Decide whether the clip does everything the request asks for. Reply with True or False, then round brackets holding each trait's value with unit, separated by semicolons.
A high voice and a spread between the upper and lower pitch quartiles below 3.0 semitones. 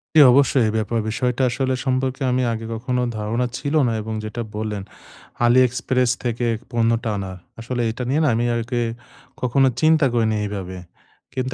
False (120 Hz; 2.4 semitones)